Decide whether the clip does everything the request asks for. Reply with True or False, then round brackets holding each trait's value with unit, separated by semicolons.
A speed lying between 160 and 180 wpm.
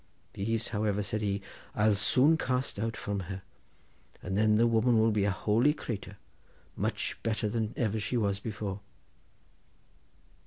False (150 wpm)